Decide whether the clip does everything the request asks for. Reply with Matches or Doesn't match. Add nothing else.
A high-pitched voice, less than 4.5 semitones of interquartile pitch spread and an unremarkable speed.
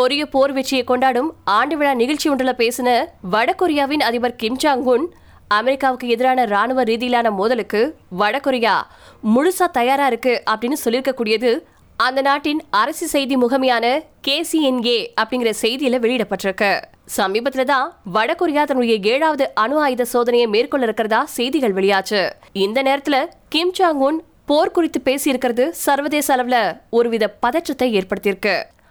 Matches